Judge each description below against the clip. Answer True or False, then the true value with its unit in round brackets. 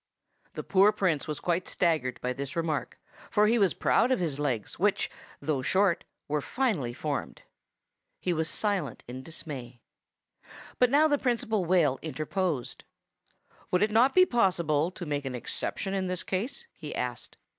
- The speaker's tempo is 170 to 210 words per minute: False (160 wpm)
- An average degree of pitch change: False (6.1 semitones)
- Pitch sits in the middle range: True (175 Hz)